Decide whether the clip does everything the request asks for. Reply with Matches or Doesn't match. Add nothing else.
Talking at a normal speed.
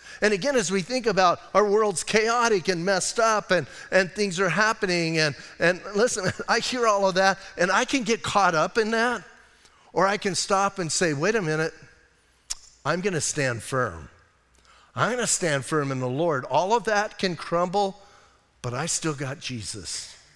Matches